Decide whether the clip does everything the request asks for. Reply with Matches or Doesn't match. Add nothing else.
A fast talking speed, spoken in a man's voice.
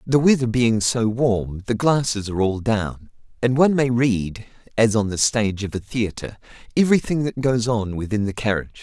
Doesn't match